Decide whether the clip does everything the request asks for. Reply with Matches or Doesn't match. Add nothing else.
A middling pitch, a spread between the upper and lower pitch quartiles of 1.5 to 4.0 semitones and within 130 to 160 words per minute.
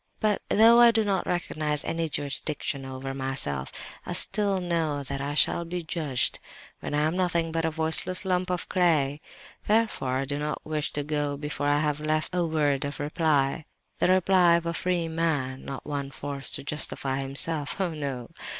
Doesn't match